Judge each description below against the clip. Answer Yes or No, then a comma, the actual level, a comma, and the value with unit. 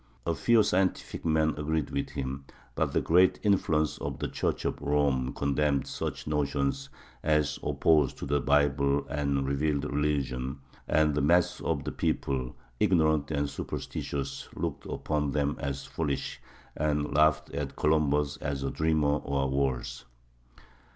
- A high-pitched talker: No, very low, 75 Hz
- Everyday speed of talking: Yes, average, 145 wpm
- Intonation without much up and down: Yes, narrow, 1.9 semitones